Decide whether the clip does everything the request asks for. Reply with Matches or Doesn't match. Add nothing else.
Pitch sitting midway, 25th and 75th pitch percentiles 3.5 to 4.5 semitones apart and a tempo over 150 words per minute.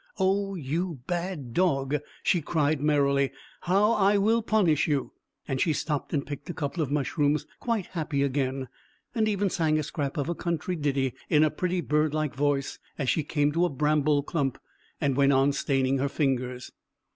Matches